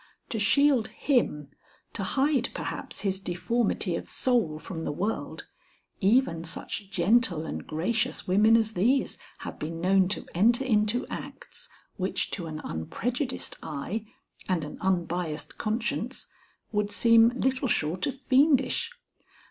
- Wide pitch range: Yes, wide, 5.9 semitones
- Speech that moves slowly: Yes, slow, 130 wpm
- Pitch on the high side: Yes, high, 210 Hz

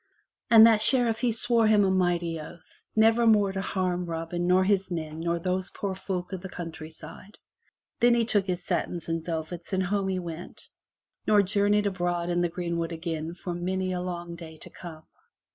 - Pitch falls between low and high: Yes, medium, 180 Hz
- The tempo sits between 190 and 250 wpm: Yes, average, 195 wpm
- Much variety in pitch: No, average, 2.9 semitones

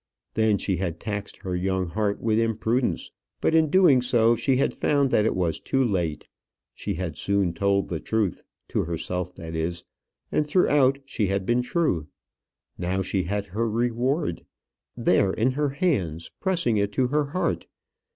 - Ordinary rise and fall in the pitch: No, wide, 5.8 semitones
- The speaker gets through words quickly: No, average, 170 wpm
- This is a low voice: Yes, low, 105 Hz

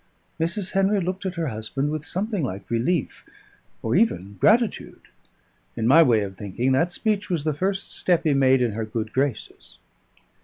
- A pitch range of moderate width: No, wide, 8.1 semitones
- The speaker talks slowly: No, average, 175 wpm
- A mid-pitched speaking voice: Yes, medium, 150 Hz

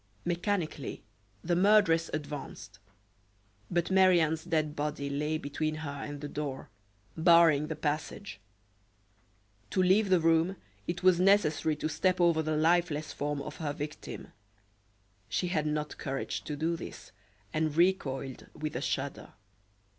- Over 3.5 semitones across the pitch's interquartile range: No, average, 2.8 semitones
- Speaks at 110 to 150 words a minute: Yes, average, 140 wpm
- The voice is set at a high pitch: No, medium, 155 Hz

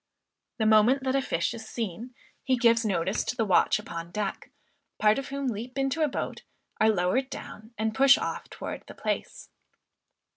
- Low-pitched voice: No, high, 230 Hz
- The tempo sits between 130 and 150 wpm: No, average, 180 wpm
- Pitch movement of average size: Yes, average, 3.7 semitones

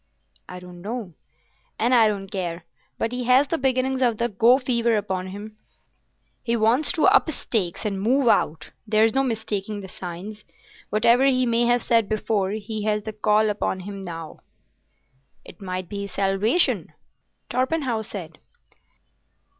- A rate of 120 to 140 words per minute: No, average, 155 wpm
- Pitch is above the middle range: Yes, high, 215 Hz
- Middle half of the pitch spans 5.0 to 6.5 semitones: No, average, 3.7 semitones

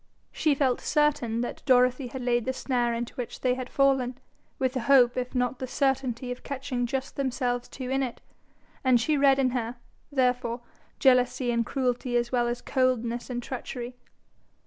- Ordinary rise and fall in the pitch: No, narrow, 1.6 semitones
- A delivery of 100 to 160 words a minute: No, average, 175 wpm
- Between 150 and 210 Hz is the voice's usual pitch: No, very high, 250 Hz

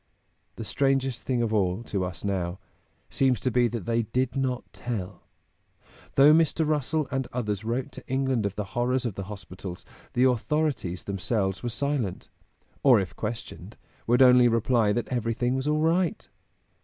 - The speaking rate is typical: Yes, average, 165 wpm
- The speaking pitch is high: No, low, 120 Hz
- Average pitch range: Yes, average, 4.2 semitones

